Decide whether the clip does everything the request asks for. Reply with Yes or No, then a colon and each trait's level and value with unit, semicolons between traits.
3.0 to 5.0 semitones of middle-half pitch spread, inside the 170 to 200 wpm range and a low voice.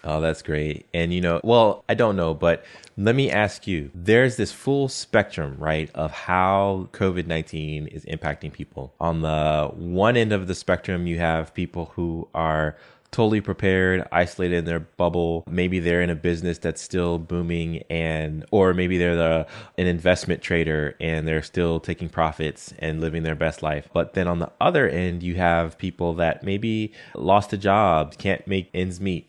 No: narrow, 2.6 semitones; average, 180 wpm; very low, 85 Hz